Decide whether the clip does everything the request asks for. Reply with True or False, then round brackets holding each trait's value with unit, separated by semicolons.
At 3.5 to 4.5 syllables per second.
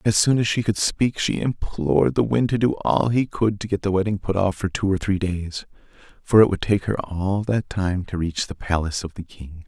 False (5.1 syllables/s)